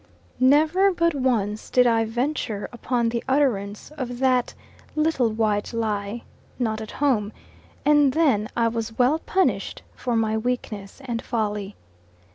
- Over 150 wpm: No, slow, 135 wpm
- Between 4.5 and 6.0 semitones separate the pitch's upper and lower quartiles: No, average, 3.6 semitones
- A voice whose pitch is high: Yes, high, 235 Hz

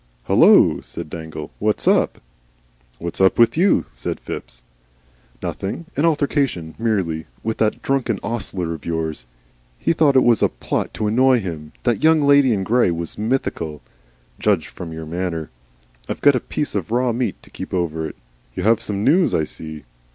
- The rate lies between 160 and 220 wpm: Yes, average, 175 wpm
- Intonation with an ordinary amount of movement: No, wide, 7.7 semitones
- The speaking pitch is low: Yes, low, 105 Hz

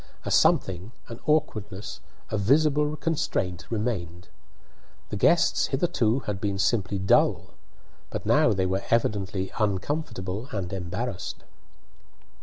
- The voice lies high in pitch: No, low, 105 Hz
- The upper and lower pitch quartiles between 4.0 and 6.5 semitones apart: Yes, average, 4.6 semitones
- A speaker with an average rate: No, slow, 110 wpm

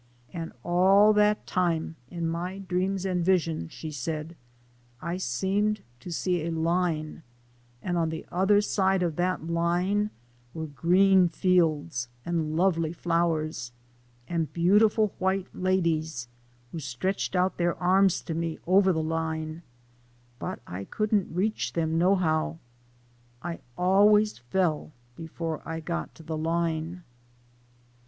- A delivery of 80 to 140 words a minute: Yes, slow, 135 wpm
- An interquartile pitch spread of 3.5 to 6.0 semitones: No, average, 2.8 semitones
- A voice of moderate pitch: Yes, medium, 170 Hz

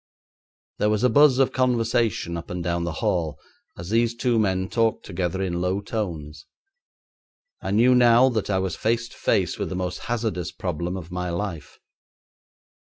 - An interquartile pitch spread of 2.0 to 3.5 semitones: No, average, 4.8 semitones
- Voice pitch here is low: Yes, very low, 95 Hz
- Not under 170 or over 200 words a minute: Yes, average, 175 wpm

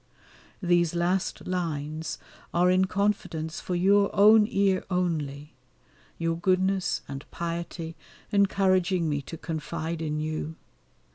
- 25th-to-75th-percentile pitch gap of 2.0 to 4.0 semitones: Yes, average, 3.0 semitones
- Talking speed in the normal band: No, slow, 115 wpm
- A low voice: No, medium, 175 Hz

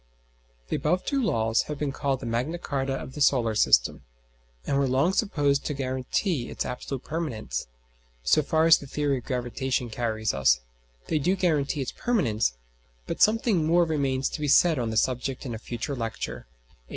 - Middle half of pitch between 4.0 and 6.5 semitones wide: Yes, average, 4.4 semitones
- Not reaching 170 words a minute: No, average, 185 wpm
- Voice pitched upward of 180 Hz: No, low, 135 Hz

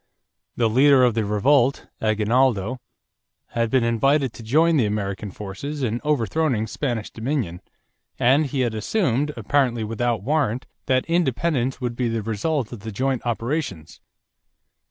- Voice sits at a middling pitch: No, low, 120 Hz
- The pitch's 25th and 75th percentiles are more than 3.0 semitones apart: Yes, average, 4.1 semitones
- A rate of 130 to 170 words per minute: Yes, average, 140 wpm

